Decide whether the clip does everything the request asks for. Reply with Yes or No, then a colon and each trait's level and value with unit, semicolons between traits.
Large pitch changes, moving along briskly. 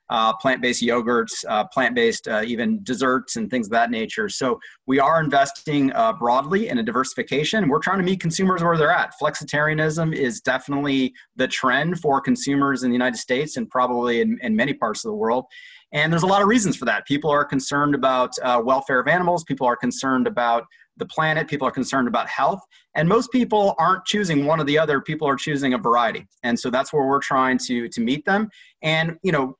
Yes: wide, 7.1 semitones; fast, 210 wpm